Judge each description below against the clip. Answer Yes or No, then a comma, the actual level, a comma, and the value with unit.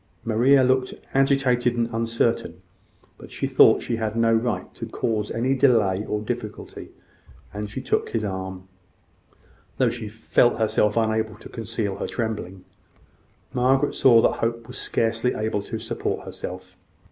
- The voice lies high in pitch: No, low, 115 Hz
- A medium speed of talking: Yes, average, 145 wpm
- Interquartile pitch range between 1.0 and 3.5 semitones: Yes, narrow, 2.5 semitones